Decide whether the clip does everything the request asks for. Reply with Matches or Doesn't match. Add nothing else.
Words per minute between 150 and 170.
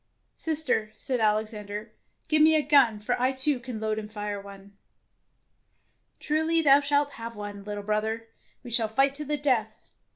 Matches